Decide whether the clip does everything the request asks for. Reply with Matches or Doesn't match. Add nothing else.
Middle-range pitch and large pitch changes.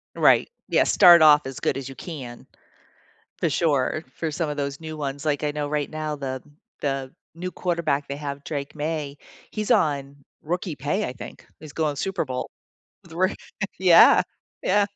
Doesn't match